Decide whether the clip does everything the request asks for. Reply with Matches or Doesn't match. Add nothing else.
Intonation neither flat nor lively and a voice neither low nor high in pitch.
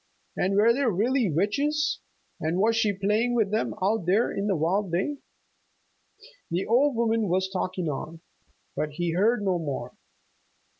Doesn't match